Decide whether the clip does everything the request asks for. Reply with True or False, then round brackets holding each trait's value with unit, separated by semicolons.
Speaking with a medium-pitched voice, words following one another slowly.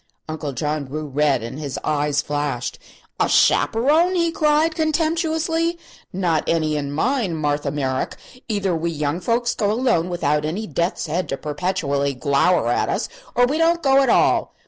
False (165 Hz; 165 wpm)